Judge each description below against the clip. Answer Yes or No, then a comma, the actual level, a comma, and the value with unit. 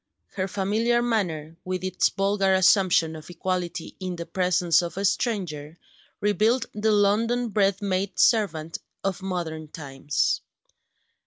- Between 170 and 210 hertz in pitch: Yes, medium, 185 Hz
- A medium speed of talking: No, slow, 130 wpm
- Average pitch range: Yes, average, 3.4 semitones